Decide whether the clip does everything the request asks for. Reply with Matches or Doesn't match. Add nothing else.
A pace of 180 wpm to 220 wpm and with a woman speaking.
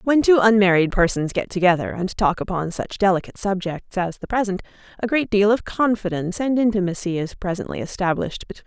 Matches